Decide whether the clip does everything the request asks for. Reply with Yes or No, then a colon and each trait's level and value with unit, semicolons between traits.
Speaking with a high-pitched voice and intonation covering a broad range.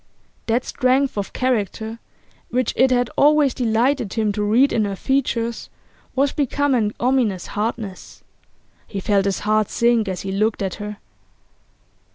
No: high, 230 Hz; average, 3.6 semitones